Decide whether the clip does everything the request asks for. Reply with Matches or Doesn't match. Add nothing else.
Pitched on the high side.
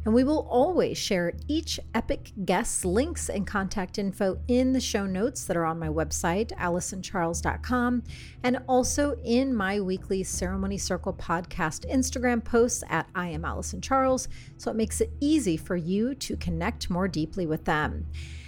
Matches